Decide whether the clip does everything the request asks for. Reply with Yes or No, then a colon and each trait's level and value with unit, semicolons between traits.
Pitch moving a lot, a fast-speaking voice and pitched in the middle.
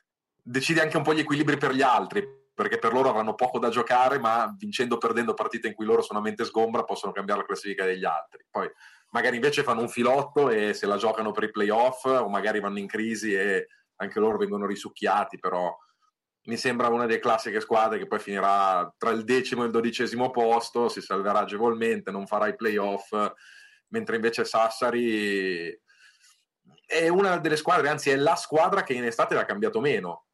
No: wide, 5.7 semitones; fast, 195 wpm; low, 120 Hz